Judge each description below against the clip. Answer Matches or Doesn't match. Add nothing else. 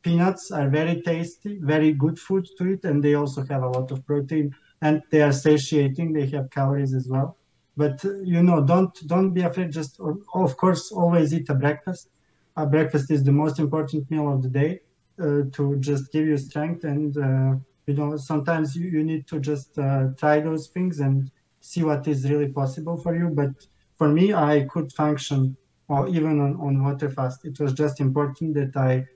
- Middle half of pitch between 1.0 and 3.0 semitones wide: Matches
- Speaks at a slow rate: Doesn't match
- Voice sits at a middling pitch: Matches